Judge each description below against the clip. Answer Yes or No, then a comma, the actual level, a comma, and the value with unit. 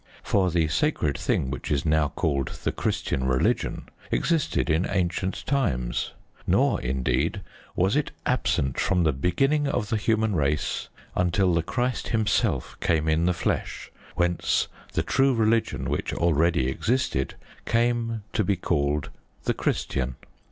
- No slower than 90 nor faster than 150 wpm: Yes, average, 140 wpm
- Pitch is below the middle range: Yes, very low, 85 Hz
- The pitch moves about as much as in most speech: No, wide, 7.3 semitones